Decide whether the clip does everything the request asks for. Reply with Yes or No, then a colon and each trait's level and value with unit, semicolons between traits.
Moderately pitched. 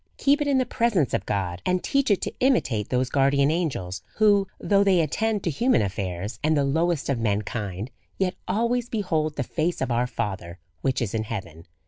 Yes: medium, 145 Hz